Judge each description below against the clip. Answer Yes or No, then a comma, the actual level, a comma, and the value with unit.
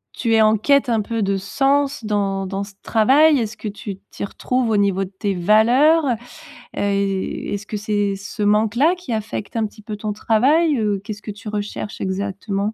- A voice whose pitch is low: No, high, 215 Hz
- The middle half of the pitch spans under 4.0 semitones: Yes, average, 2.8 semitones